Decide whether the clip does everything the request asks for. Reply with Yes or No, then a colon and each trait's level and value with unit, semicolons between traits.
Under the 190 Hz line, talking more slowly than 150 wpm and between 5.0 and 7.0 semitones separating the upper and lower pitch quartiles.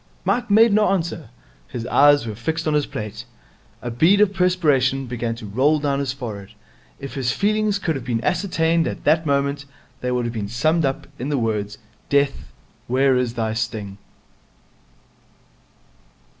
No: low, 135 Hz; average, 165 wpm; wide, 5.5 semitones